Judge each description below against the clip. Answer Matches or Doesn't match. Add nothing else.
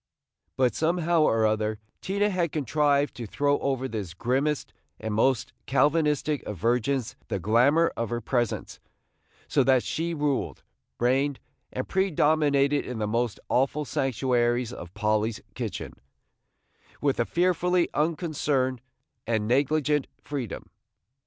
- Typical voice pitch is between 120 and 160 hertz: Matches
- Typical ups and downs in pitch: Matches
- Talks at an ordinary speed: Doesn't match